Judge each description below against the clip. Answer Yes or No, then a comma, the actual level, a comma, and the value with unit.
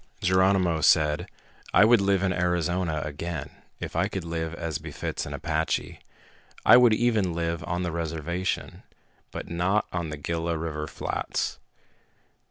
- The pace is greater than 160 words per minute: No, average, 145 wpm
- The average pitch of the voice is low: Yes, very low, 85 Hz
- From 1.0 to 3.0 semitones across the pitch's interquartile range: Yes, narrow, 2.5 semitones